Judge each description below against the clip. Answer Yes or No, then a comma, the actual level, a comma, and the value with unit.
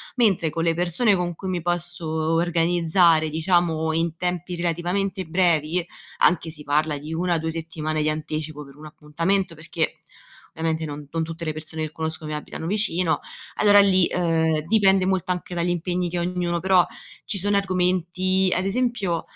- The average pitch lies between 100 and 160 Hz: No, medium, 170 Hz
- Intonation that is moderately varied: No, narrow, 2.3 semitones